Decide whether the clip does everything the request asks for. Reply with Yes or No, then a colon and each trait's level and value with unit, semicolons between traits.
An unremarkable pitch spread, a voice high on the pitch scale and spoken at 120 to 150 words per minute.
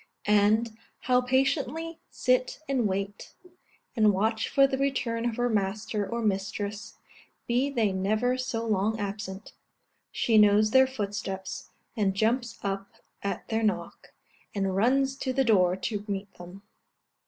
Yes: average, 3.9 semitones; high, 220 Hz; average, 140 wpm